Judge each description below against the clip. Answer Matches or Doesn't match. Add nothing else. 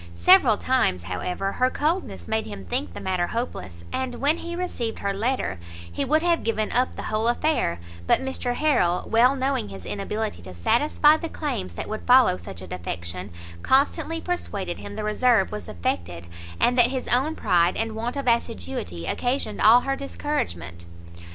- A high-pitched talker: Matches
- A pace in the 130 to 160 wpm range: Doesn't match